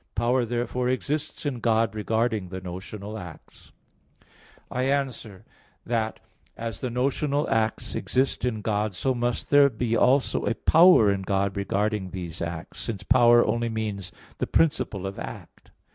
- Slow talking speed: No, average, 145 wpm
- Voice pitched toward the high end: No, low, 115 Hz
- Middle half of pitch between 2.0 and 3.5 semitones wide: No, average, 4.0 semitones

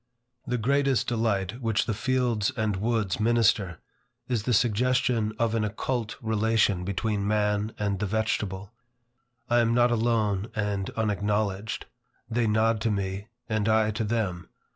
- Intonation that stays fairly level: Yes, narrow, 2.3 semitones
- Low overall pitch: Yes, low, 110 Hz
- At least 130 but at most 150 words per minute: Yes, average, 140 wpm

